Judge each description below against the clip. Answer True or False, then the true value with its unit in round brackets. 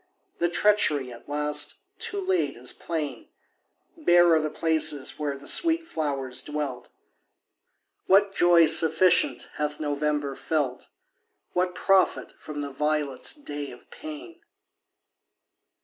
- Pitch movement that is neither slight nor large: True (4.0 semitones)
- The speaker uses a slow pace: True (115 wpm)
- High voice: False (155 Hz)